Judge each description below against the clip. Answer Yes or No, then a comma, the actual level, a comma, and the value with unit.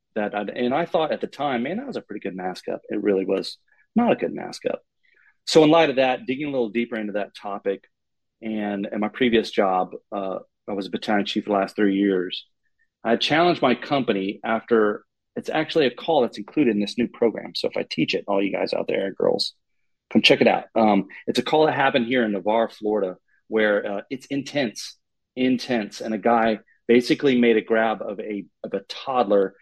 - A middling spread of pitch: Yes, average, 4.0 semitones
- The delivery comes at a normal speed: No, fast, 220 wpm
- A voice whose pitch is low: Yes, low, 110 Hz